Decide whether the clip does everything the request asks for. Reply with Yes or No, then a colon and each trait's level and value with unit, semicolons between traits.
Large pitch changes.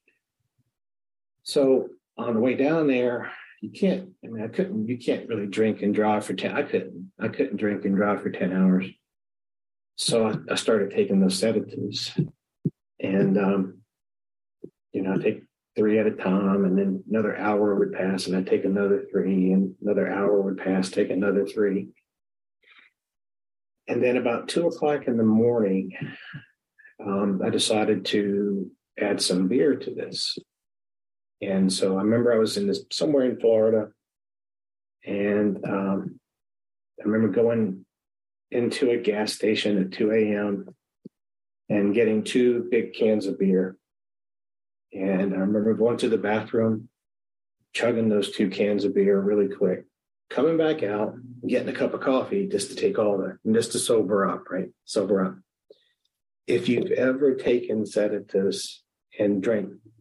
No: average, 3.8 semitones